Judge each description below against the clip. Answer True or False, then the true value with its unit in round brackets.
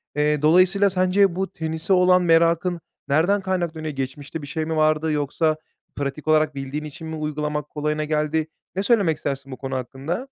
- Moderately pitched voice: True (155 Hz)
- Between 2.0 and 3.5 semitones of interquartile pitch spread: True (2.9 semitones)